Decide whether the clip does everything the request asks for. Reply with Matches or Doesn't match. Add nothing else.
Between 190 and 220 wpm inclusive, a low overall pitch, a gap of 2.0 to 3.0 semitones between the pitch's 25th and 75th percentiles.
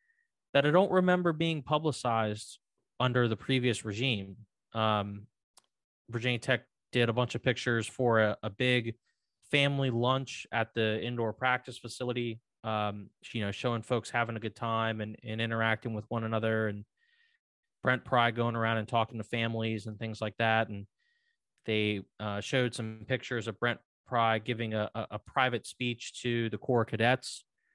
Doesn't match